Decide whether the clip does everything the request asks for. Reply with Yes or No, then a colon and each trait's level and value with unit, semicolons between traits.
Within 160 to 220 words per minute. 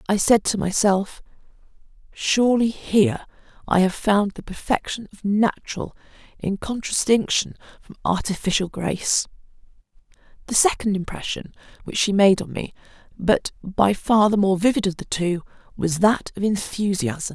No: slow, 135 wpm